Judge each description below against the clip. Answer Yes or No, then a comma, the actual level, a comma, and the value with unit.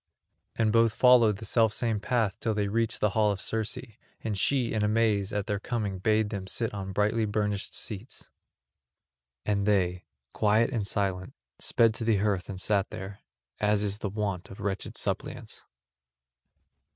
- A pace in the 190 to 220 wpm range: No, average, 165 wpm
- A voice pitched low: Yes, low, 105 Hz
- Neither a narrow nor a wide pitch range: No, narrow, 2.0 semitones